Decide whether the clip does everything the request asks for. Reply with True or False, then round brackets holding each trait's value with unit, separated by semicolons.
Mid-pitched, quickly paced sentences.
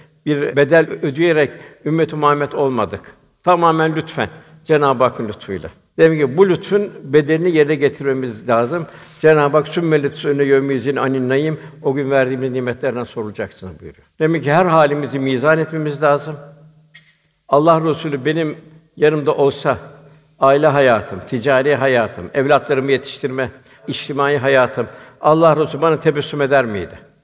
False (145 Hz; 125 wpm)